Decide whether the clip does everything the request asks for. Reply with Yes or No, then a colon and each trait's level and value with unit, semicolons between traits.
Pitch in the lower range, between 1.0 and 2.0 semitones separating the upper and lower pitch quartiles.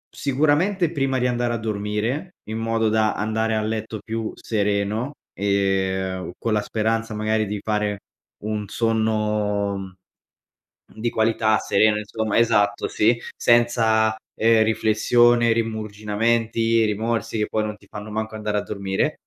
Yes: low, 110 Hz; narrow, 1.5 semitones